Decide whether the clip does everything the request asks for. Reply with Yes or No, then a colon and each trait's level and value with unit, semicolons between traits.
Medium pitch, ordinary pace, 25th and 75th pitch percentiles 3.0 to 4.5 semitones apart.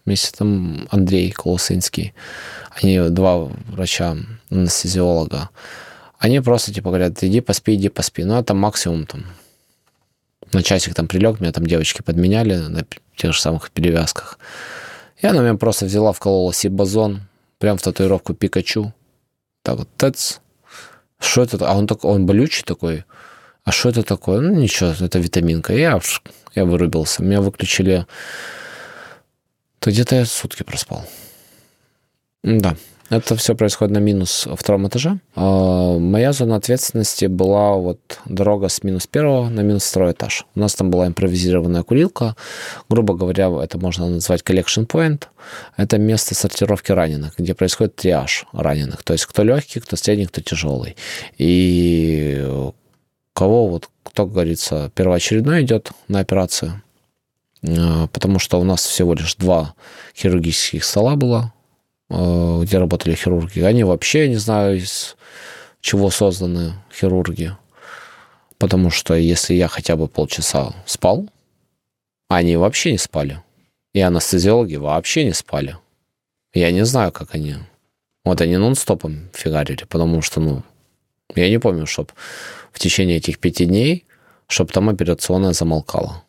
No: very low, 95 Hz; average, 140 wpm; average, 3.7 semitones